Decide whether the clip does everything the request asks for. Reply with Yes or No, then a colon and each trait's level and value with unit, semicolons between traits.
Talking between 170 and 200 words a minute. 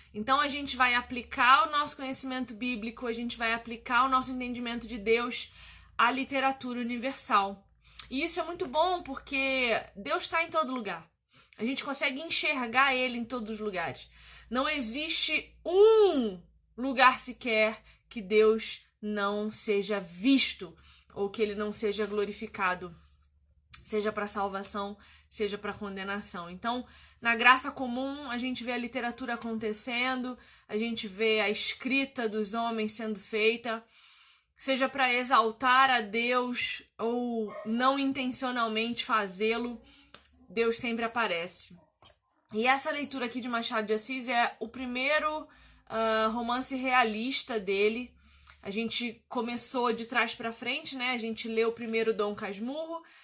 No: average, 140 wpm